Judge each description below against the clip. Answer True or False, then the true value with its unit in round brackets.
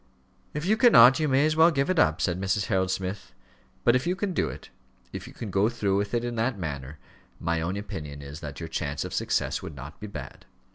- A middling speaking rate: False (240 wpm)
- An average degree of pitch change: False (8.5 semitones)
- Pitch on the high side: False (100 Hz)